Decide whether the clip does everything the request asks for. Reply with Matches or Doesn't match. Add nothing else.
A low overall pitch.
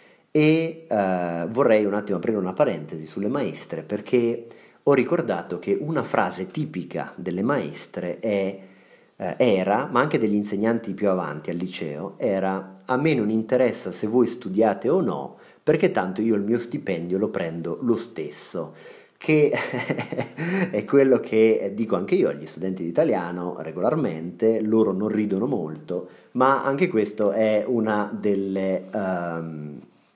Matches